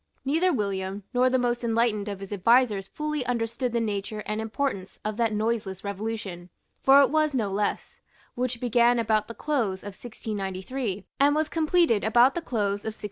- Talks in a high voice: Yes, high, 225 Hz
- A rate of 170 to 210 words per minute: Yes, average, 180 wpm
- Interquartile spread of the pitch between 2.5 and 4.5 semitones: Yes, average, 3.9 semitones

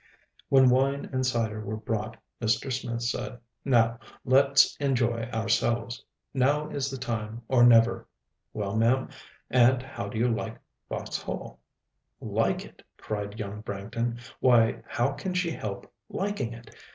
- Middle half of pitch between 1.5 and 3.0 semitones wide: Yes, average, 2.7 semitones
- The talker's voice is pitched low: Yes, low, 120 Hz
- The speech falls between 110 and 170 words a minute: Yes, average, 140 wpm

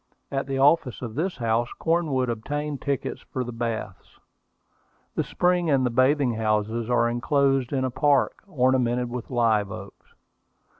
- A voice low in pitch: Yes, low, 130 Hz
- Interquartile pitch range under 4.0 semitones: Yes, average, 3.1 semitones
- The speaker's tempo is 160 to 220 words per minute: No, average, 150 wpm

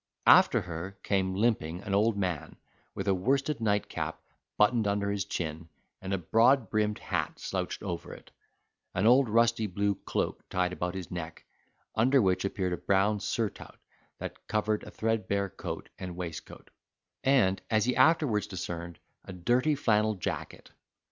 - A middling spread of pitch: Yes, average, 3.5 semitones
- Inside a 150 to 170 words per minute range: Yes, average, 155 wpm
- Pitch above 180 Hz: No, low, 100 Hz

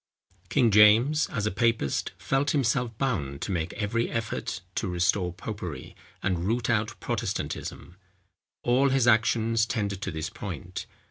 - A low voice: Yes, low, 110 Hz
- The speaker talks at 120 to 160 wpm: Yes, average, 140 wpm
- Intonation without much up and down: No, average, 4.3 semitones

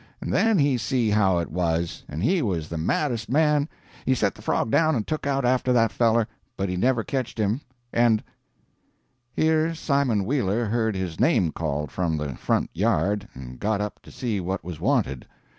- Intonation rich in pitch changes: Yes, wide, 6.4 semitones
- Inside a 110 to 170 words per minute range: No, average, 195 wpm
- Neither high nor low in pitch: No, low, 110 Hz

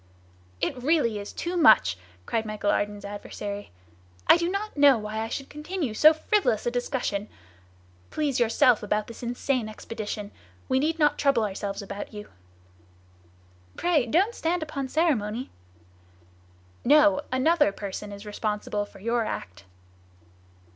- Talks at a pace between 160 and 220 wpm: No, slow, 135 wpm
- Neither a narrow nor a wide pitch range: No, wide, 6.4 semitones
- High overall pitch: Yes, high, 240 Hz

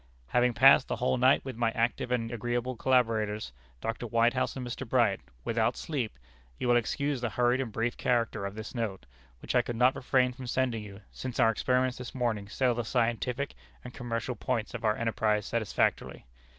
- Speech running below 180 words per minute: No, average, 190 wpm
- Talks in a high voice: No, low, 120 Hz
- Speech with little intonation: Yes, narrow, 2.0 semitones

